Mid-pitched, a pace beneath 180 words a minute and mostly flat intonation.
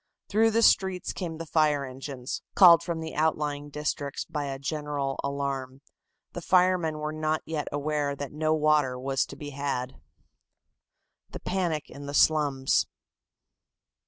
Yes: medium, 150 Hz; average, 150 wpm; narrow, 2.3 semitones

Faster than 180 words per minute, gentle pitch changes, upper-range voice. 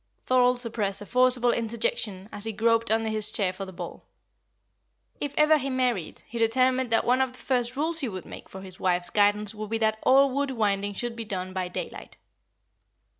No: average, 200 wpm; average, 4.0 semitones; high, 225 Hz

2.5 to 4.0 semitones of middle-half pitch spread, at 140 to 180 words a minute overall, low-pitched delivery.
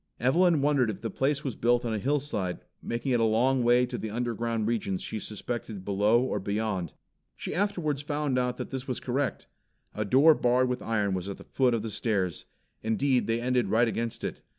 No: average, 3.4 semitones; fast, 205 wpm; low, 120 Hz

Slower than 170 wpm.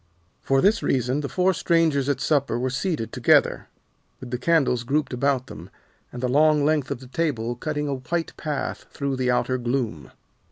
No: average, 185 wpm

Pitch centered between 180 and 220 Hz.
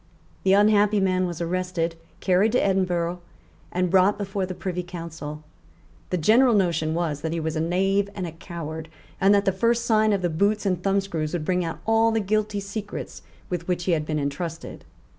Yes: medium, 185 Hz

